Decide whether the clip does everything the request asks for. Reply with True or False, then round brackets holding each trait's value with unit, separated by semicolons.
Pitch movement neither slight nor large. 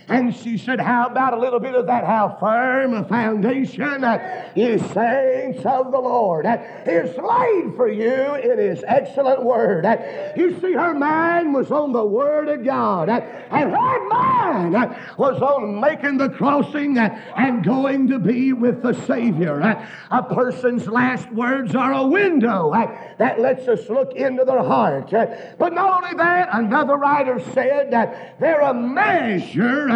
True (3.4 semitones)